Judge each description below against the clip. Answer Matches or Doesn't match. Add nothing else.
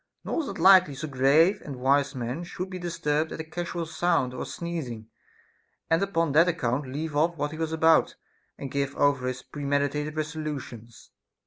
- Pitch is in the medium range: Matches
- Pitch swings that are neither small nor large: Matches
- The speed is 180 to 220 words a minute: Matches